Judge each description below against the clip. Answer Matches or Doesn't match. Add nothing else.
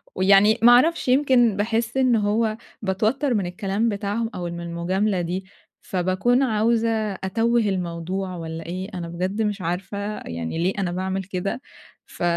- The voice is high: Matches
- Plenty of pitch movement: Doesn't match